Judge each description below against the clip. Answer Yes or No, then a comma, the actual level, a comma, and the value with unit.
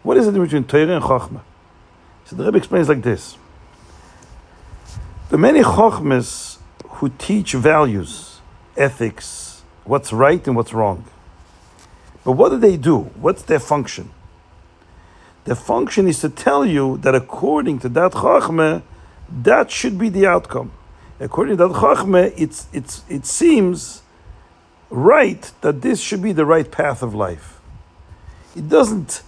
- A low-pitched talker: Yes, low, 125 Hz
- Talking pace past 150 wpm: No, average, 145 wpm